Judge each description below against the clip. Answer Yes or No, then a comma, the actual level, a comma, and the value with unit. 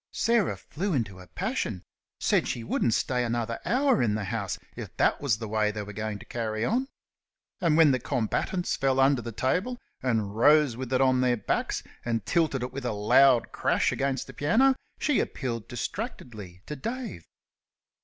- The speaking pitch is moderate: No, low, 125 Hz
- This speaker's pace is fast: No, average, 185 wpm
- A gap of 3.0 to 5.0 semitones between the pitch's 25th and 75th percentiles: No, wide, 5.6 semitones